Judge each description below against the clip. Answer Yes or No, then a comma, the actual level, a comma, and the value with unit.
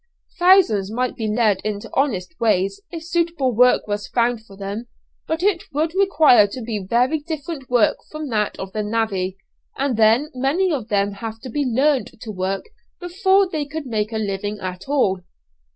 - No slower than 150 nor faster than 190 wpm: Yes, average, 180 wpm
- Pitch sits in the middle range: No, high, 240 Hz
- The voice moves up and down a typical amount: No, wide, 6.6 semitones